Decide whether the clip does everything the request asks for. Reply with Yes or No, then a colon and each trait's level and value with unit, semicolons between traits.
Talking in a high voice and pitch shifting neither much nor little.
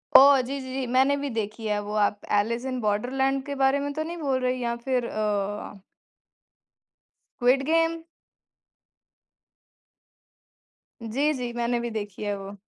Yes: very high, 250 Hz; average, 4.1 semitones